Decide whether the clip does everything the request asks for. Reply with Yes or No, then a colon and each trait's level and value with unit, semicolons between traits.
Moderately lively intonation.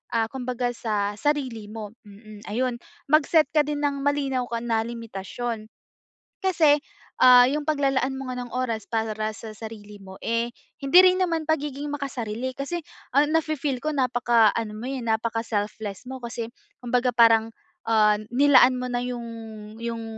Yes: average, 3.8 semitones